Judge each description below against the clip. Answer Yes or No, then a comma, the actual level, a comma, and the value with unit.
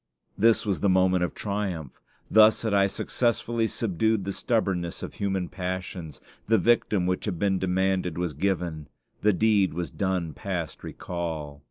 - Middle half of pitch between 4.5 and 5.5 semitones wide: No, average, 2.9 semitones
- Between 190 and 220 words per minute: No, average, 155 wpm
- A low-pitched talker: Yes, very low, 95 Hz